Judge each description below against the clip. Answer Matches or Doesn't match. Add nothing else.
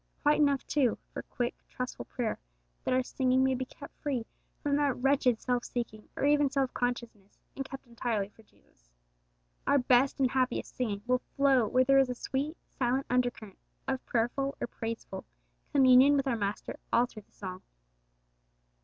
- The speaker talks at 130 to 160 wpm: Doesn't match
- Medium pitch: Doesn't match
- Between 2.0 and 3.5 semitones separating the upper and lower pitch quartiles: Matches